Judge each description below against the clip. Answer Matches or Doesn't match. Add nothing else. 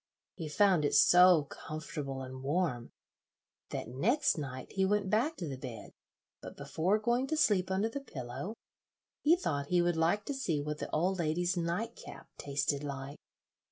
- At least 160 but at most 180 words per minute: Matches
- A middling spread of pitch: Doesn't match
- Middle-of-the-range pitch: Matches